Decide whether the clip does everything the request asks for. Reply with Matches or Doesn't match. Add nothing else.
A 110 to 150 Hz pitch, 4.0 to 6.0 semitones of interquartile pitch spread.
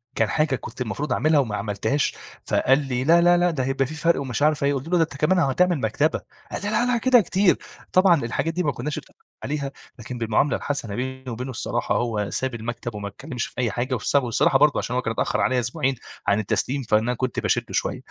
Matches